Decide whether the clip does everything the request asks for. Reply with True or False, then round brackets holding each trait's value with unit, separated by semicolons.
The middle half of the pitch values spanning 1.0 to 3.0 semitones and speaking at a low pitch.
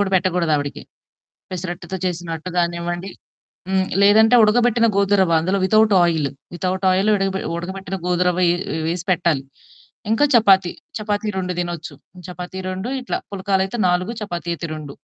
False (2.4 semitones; 185 Hz)